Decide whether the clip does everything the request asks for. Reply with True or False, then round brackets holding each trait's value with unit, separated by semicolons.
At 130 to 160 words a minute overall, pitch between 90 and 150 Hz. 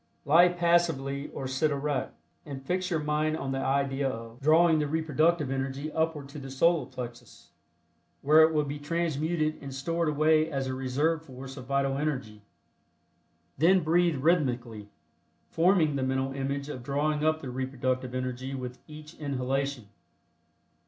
True (150 wpm; 140 Hz)